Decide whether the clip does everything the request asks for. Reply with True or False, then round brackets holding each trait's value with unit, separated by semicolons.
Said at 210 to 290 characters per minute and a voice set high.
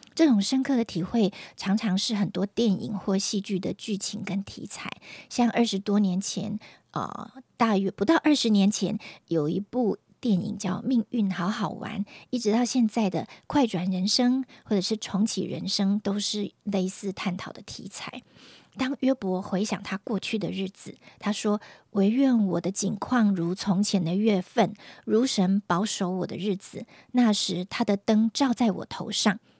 True (240 characters per minute; 205 Hz)